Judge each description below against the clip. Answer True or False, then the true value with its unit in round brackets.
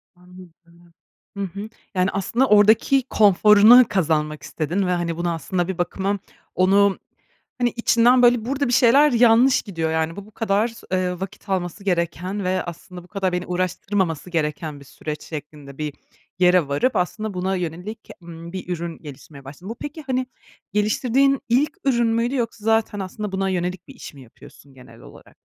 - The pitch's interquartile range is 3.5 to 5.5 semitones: True (4.7 semitones)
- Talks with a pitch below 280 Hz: True (190 Hz)